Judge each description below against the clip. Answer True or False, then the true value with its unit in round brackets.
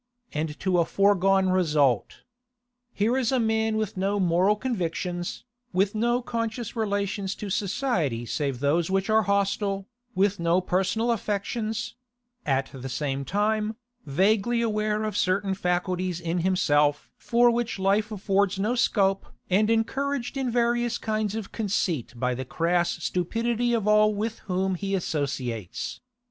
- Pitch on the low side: False (195 Hz)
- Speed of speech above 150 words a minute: False (140 wpm)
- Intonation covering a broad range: False (3.9 semitones)